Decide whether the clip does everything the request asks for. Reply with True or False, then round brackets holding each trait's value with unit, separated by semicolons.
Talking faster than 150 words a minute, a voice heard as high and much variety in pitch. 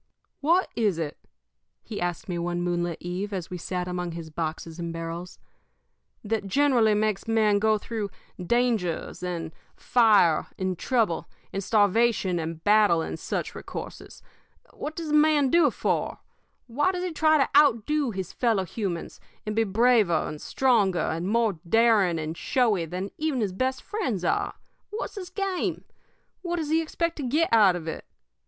True (165 wpm; 210 Hz; 6.7 semitones)